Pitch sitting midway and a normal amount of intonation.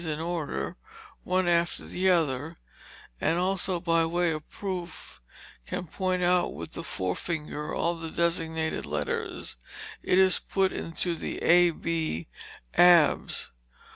No: medium, 170 Hz; narrow, 1.9 semitones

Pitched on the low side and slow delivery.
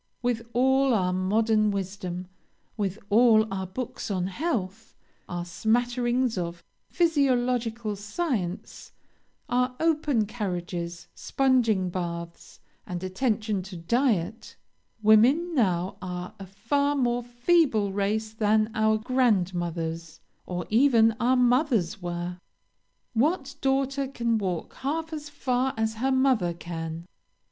No: high, 220 Hz; slow, 115 wpm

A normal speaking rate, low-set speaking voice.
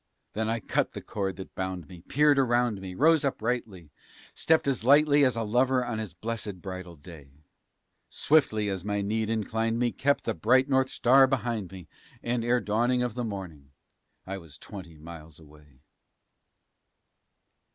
Yes: average, 160 wpm; low, 110 Hz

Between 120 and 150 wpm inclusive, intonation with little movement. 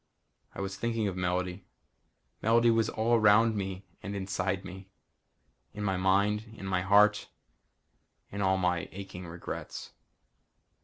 Yes: slow, 135 wpm; narrow, 2.1 semitones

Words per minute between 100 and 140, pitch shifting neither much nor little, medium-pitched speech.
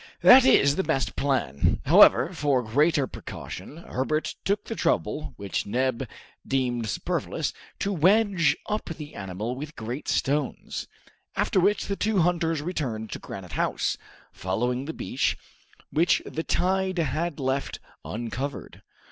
No: slow, 135 wpm; wide, 5.8 semitones; medium, 145 Hz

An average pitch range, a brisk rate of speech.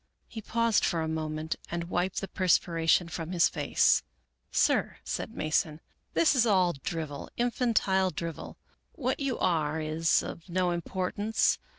No: average, 4.0 semitones; average, 155 wpm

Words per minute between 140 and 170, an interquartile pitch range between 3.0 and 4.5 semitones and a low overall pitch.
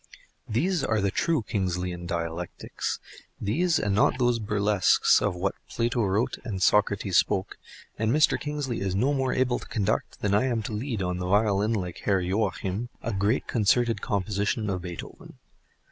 Yes: average, 165 wpm; average, 3.9 semitones; low, 105 Hz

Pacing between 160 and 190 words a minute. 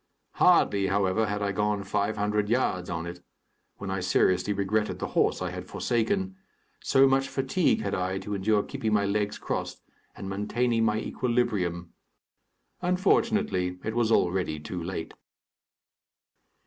No: average, 145 wpm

